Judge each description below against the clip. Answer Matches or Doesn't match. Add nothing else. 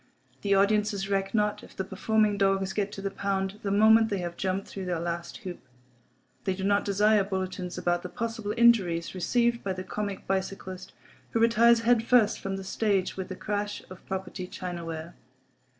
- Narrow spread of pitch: Matches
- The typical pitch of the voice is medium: Doesn't match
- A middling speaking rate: Matches